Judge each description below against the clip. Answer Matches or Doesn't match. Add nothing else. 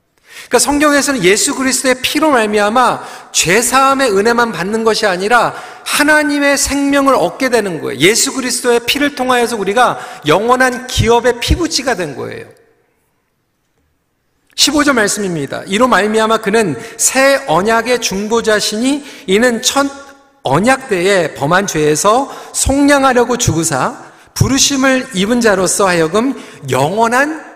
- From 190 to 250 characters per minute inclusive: Doesn't match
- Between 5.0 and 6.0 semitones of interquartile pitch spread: Doesn't match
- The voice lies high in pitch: Matches